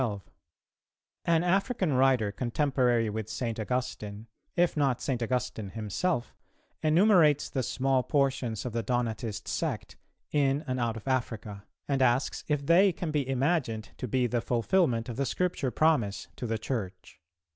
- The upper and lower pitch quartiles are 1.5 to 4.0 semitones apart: No, average, 4.4 semitones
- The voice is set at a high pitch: No, low, 125 Hz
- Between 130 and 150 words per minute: Yes, average, 145 wpm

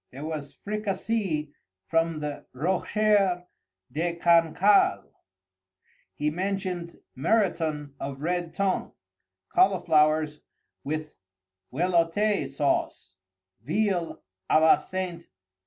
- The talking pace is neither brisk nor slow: No, slow, 85 wpm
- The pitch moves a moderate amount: Yes, average, 3.9 semitones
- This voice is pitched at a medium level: Yes, medium, 170 Hz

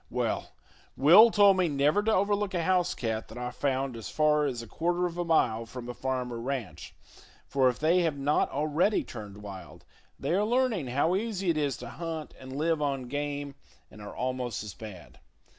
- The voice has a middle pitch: Yes, medium, 145 Hz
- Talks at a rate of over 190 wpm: Yes, average, 200 wpm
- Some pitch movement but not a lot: No, wide, 5.9 semitones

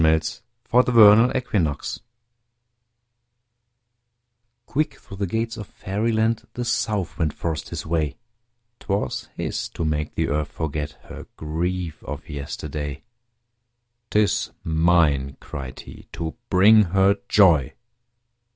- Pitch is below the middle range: Yes, very low, 85 Hz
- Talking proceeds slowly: Yes, slow, 115 wpm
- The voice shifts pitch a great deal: Yes, wide, 5.7 semitones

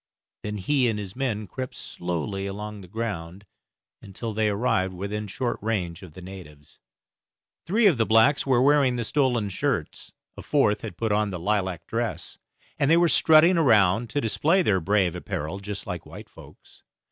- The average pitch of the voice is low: Yes, low, 105 Hz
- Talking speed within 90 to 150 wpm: No, average, 175 wpm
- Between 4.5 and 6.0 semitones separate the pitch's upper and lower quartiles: Yes, average, 5.0 semitones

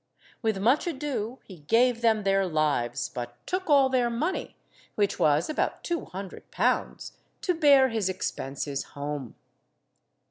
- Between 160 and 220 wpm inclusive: No, average, 140 wpm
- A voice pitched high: Yes, high, 215 Hz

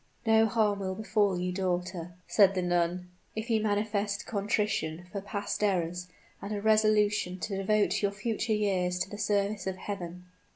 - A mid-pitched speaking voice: No, high, 200 Hz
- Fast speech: No, average, 165 wpm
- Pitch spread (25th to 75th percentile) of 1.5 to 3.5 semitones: Yes, average, 2.7 semitones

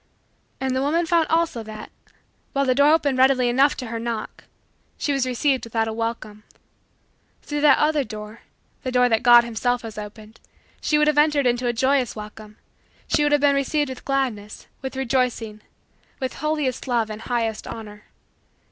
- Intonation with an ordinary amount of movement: Yes, average, 4.0 semitones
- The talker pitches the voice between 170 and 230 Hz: No, very high, 250 Hz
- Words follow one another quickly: No, average, 175 wpm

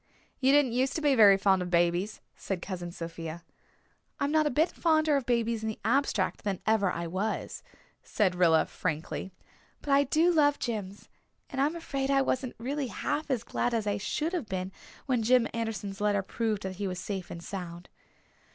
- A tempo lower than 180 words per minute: No, average, 190 wpm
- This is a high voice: Yes, high, 220 Hz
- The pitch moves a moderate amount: No, wide, 6.5 semitones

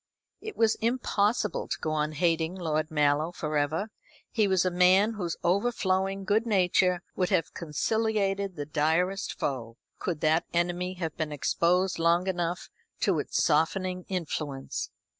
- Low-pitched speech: No, medium, 180 Hz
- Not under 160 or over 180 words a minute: No, average, 145 wpm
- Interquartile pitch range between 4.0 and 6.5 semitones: No, average, 3.5 semitones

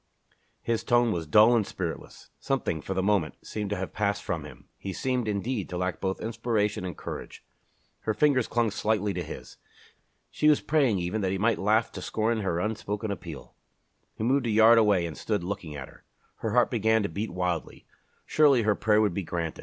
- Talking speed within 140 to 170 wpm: No, average, 200 wpm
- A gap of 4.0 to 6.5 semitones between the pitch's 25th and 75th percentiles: No, average, 3.5 semitones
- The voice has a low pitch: Yes, low, 105 Hz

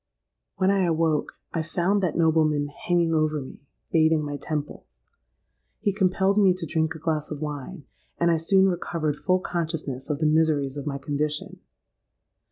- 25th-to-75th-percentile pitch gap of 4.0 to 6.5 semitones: No, average, 2.7 semitones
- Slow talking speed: No, average, 165 wpm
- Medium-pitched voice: Yes, medium, 160 Hz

